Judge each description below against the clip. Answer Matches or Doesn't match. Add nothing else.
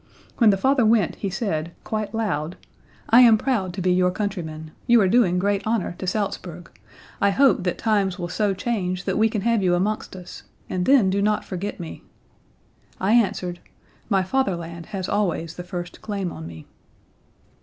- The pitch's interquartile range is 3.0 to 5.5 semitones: Matches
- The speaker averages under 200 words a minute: Matches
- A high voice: Matches